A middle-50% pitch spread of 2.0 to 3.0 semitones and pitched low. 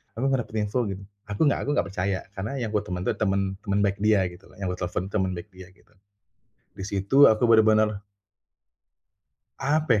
Yes: narrow, 2.4 semitones; low, 105 Hz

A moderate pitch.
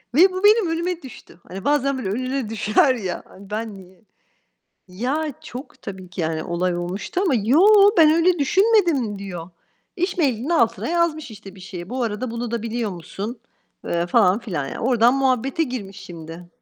No: high, 235 Hz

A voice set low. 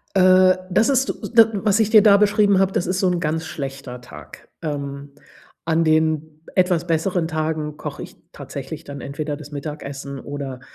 No: medium, 160 Hz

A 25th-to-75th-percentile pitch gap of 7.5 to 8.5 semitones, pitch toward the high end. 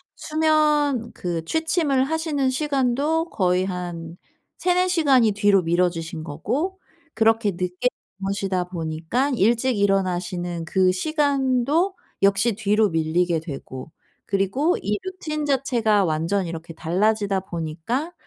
Yes: wide, 7.8 semitones; high, 205 Hz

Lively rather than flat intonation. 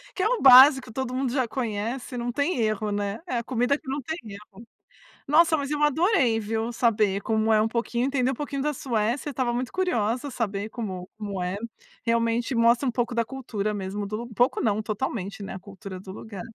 No: average, 3.8 semitones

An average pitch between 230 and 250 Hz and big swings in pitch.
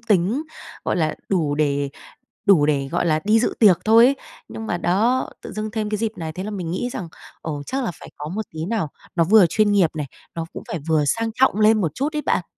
No: high, 195 Hz; wide, 5.8 semitones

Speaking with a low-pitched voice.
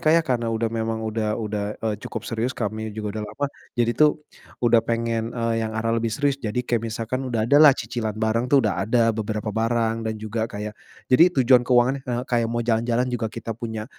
Yes: low, 115 Hz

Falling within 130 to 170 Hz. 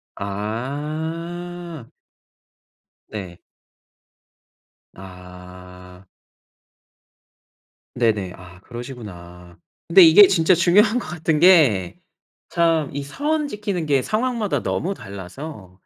Yes: medium, 140 Hz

